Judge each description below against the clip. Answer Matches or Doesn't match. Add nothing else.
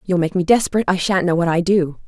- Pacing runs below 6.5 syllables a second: Doesn't match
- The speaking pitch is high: Doesn't match